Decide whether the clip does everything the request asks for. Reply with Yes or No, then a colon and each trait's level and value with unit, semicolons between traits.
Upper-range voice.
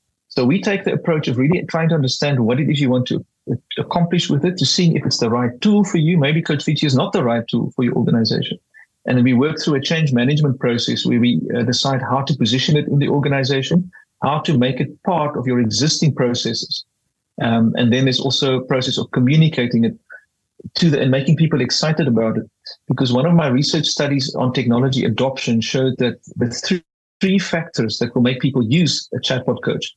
No: low, 135 Hz